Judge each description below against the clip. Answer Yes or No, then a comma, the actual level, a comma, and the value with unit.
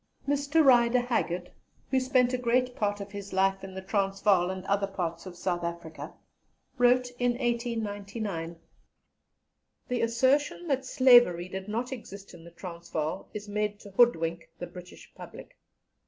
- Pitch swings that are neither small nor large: Yes, average, 5.0 semitones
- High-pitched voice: Yes, high, 205 Hz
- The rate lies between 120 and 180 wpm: Yes, average, 150 wpm